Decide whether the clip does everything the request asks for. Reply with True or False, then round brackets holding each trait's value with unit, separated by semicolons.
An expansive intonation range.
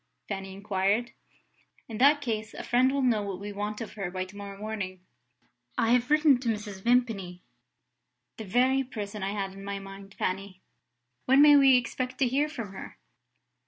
False (4.1 semitones)